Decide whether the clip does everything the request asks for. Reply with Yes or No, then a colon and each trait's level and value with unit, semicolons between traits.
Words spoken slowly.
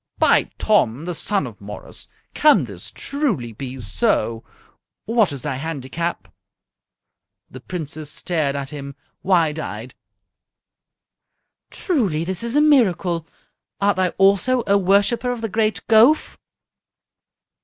Yes: slow, 120 wpm